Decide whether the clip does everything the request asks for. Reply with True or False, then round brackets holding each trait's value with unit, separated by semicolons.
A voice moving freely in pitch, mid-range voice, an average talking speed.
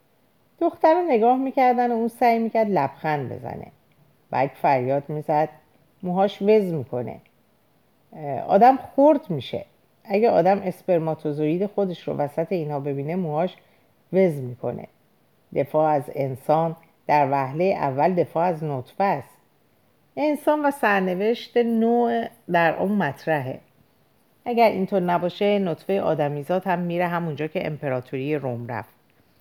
True (6.0 semitones; 165 Hz; 120 wpm)